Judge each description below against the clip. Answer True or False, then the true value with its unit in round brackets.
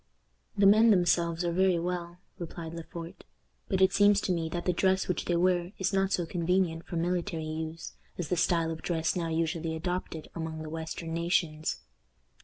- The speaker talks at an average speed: True (190 wpm)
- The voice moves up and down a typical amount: False (1.9 semitones)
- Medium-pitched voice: True (170 Hz)